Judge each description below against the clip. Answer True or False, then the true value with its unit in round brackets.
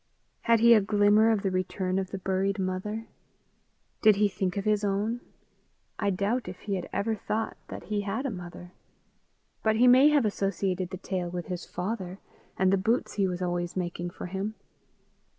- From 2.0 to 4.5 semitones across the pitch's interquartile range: True (2.7 semitones)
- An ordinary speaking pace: True (185 wpm)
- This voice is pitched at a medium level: False (195 Hz)